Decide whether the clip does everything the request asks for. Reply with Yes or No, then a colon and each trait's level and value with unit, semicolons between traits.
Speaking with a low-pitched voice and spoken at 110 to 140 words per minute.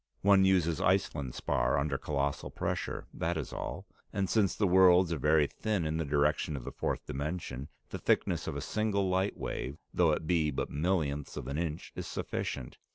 No: very low, 80 Hz; average, 190 wpm